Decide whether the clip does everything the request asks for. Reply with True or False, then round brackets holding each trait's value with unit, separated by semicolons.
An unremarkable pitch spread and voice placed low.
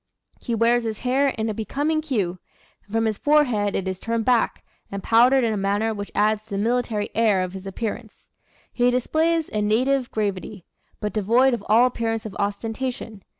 False (3.1 semitones; 225 Hz)